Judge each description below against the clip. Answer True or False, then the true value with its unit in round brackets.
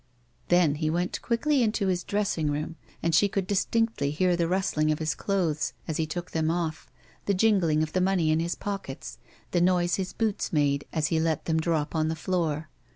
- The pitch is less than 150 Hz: False (170 Hz)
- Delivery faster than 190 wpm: True (205 wpm)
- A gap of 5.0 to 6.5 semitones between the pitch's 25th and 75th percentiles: False (3.3 semitones)